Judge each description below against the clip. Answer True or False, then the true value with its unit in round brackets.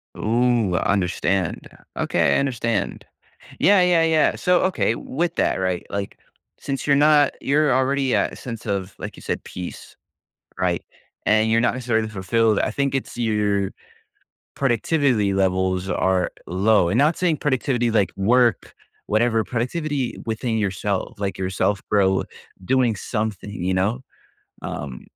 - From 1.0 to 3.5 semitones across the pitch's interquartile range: False (5.3 semitones)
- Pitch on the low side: True (110 Hz)